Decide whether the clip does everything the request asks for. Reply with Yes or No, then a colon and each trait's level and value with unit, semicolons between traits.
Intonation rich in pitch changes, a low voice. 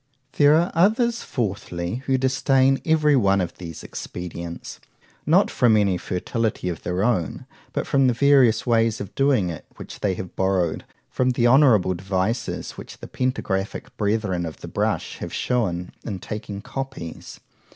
Yes: wide, 6.2 semitones; low, 110 Hz